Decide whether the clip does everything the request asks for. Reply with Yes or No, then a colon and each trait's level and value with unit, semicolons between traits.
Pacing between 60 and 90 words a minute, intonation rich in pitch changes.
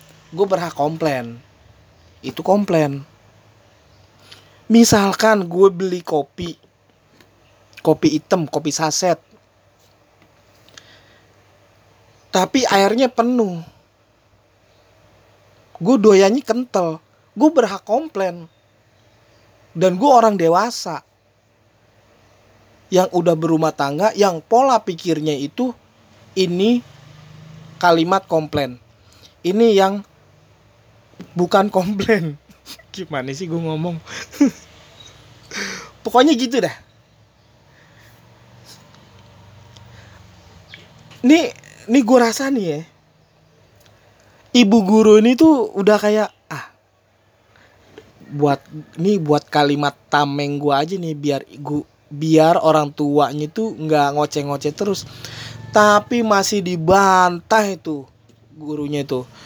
Yes: slow, 85 wpm; wide, 8.9 semitones